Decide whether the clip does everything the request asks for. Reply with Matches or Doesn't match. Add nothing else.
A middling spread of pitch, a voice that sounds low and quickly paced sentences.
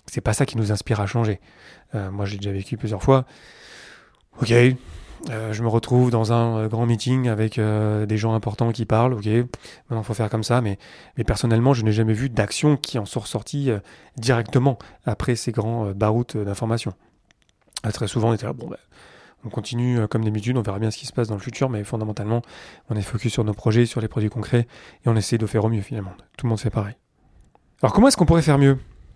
Doesn't match